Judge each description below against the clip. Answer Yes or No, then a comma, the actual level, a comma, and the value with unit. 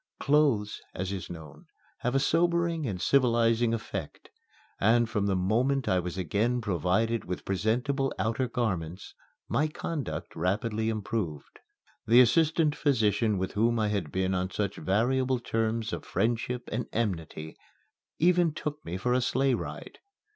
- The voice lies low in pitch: Yes, low, 115 Hz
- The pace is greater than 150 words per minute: No, average, 145 wpm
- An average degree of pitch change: Yes, average, 4.9 semitones